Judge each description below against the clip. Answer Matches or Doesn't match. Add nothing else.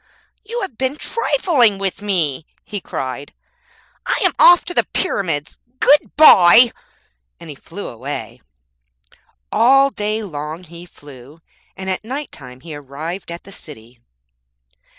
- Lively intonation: Matches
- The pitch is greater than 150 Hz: Matches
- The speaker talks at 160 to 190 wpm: Doesn't match